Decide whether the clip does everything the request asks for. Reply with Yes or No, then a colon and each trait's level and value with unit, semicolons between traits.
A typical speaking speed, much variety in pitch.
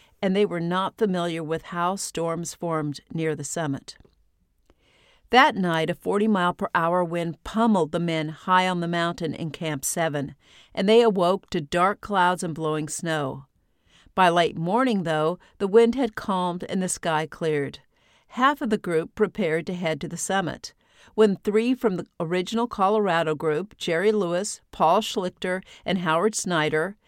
No: average, 165 wpm; average, 3.8 semitones